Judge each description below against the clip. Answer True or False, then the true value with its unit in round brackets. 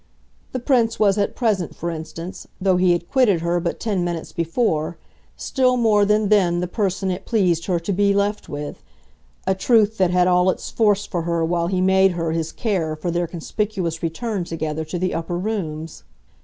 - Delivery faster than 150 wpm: True (195 wpm)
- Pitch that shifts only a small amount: False (3.4 semitones)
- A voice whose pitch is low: False (180 Hz)